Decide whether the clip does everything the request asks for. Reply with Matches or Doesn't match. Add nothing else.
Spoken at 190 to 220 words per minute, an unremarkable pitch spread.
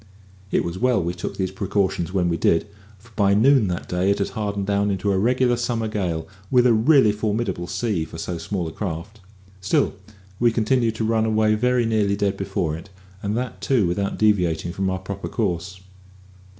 Matches